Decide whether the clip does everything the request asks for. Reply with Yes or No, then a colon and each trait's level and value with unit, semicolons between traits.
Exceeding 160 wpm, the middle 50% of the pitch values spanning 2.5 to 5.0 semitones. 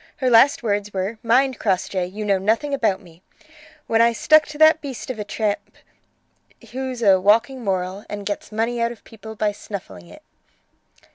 Yes: average, 180 wpm; average, 3.4 semitones